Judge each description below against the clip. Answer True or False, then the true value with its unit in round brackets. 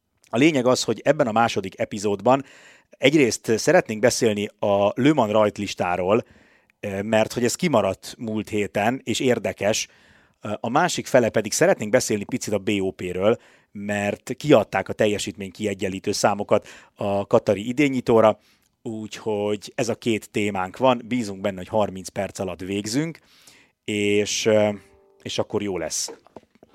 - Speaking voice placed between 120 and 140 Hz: False (105 Hz)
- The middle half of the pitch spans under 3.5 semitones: True (2.7 semitones)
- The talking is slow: False (130 wpm)